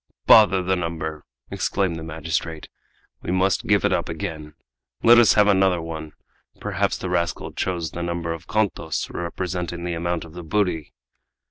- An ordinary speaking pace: Yes, average, 160 wpm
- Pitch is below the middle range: Yes, very low, 85 Hz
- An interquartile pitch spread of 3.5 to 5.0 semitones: No, narrow, 2.4 semitones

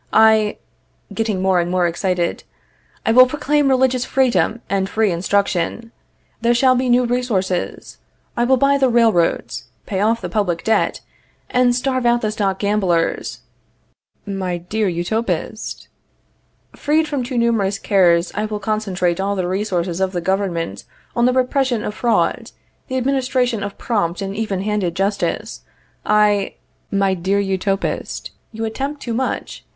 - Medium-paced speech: Yes, average, 145 wpm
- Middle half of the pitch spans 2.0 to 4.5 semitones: Yes, average, 4.2 semitones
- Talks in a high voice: Yes, high, 210 Hz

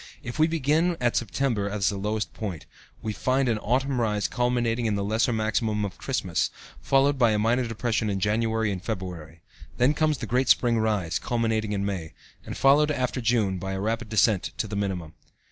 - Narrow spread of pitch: No, average, 3.5 semitones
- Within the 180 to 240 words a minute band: Yes, average, 195 wpm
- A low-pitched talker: Yes, low, 110 Hz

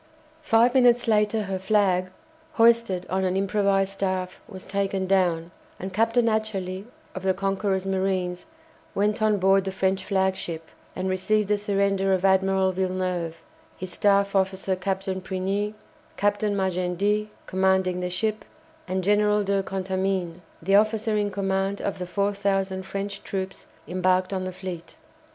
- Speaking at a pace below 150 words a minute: Yes, average, 140 wpm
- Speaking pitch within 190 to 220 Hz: Yes, high, 195 Hz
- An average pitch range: No, narrow, 1.5 semitones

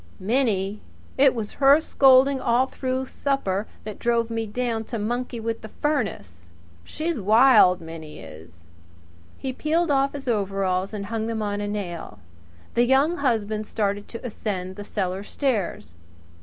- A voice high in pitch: Yes, high, 220 Hz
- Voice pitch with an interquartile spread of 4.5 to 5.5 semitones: Yes, average, 4.9 semitones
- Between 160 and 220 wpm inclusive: No, average, 150 wpm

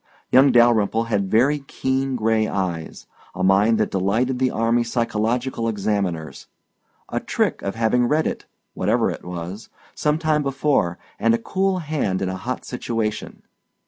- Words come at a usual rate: Yes, average, 150 wpm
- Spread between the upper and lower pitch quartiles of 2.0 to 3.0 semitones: No, average, 4.6 semitones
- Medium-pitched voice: No, low, 115 Hz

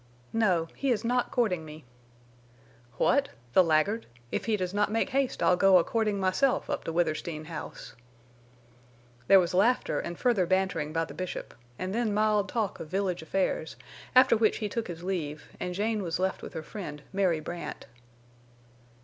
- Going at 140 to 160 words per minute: No, average, 175 wpm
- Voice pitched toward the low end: No, high, 190 Hz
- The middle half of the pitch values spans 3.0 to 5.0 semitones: Yes, average, 4.3 semitones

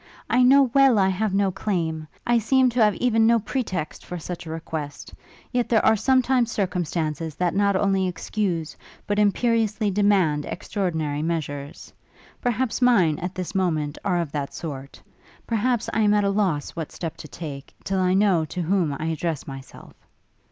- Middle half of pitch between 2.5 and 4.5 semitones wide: No, average, 5.3 semitones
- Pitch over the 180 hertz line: Yes, high, 190 Hz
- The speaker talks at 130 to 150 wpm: No, average, 175 wpm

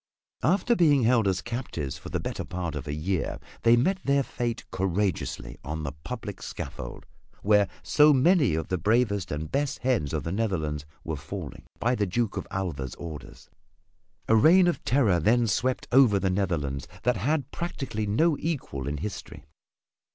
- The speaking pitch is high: No, low, 105 Hz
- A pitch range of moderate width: No, wide, 7.7 semitones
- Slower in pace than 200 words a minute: Yes, average, 175 wpm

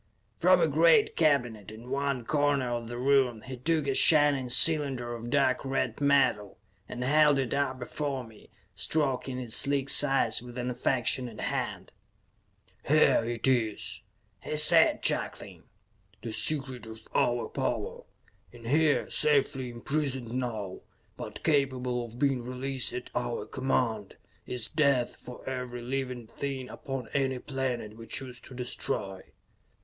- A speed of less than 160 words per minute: Yes, average, 140 wpm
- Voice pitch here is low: Yes, low, 130 Hz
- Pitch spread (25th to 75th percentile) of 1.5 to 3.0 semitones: Yes, narrow, 2.6 semitones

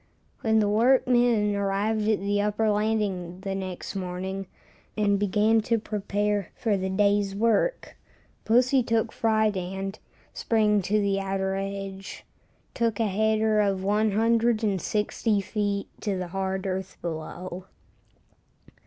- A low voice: No, high, 205 Hz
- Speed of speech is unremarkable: No, slow, 125 wpm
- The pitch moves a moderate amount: No, narrow, 2.1 semitones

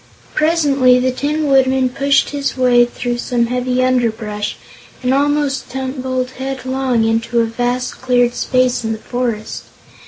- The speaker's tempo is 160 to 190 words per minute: No, slow, 135 wpm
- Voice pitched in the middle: No, very high, 255 Hz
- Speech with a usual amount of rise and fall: No, narrow, 1.7 semitones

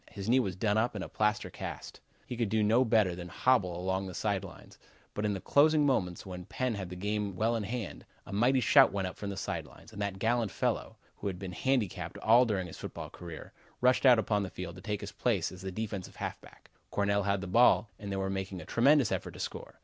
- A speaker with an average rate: No, fast, 245 wpm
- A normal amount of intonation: Yes, average, 3.4 semitones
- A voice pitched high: No, low, 100 Hz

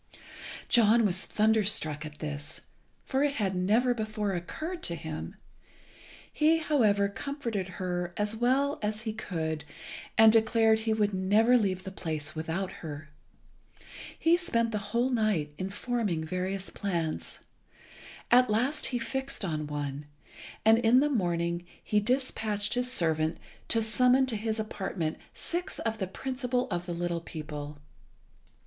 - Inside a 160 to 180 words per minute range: No, average, 140 wpm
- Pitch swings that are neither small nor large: No, wide, 5.7 semitones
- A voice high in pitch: Yes, high, 210 Hz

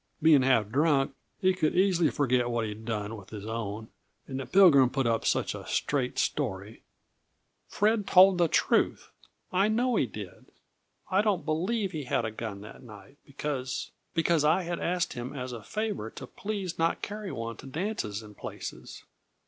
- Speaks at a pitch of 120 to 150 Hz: Yes, medium, 140 Hz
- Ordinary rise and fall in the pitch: No, wide, 8.1 semitones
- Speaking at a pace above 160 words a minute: Yes, average, 180 wpm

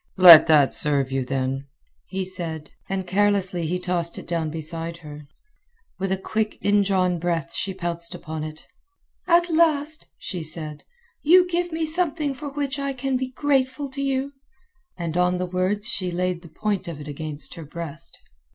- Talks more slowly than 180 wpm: Yes, average, 170 wpm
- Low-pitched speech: No, medium, 180 Hz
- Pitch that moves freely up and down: Yes, wide, 8.4 semitones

